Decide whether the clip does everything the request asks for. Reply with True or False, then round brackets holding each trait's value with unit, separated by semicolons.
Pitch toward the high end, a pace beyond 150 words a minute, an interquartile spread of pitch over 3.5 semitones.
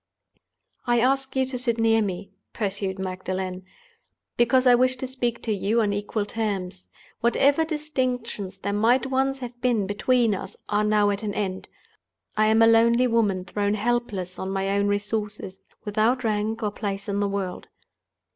False (215 Hz; 165 wpm; 3.2 semitones)